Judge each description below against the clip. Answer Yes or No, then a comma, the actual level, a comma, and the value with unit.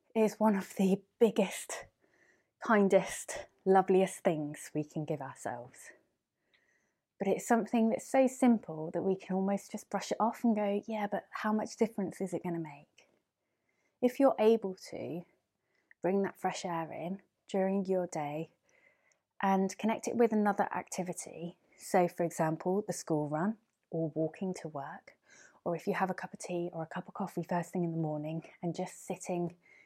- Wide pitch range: No, average, 3.7 semitones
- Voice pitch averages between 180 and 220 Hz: Yes, high, 190 Hz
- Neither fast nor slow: Yes, average, 175 wpm